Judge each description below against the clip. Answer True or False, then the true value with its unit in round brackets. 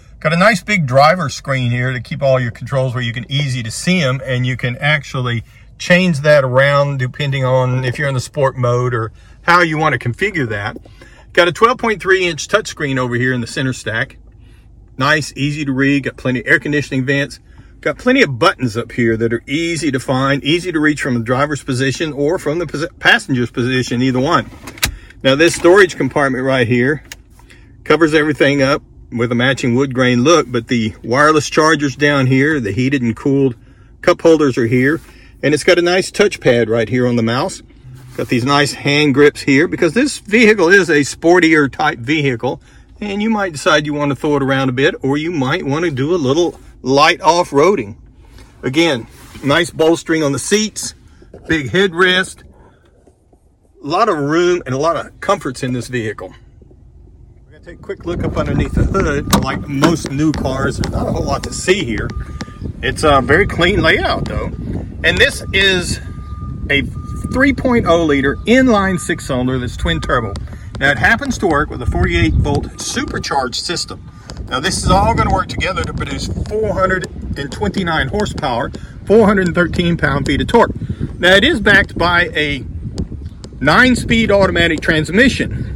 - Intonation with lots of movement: False (4.8 semitones)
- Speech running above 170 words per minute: True (185 wpm)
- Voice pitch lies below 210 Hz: True (140 Hz)